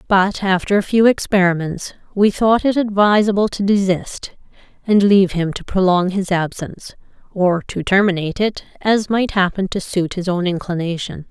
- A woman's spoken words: Yes, female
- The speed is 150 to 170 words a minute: Yes, average, 160 wpm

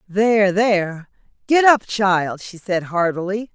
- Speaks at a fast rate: No, slow, 135 wpm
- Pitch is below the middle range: No, high, 200 Hz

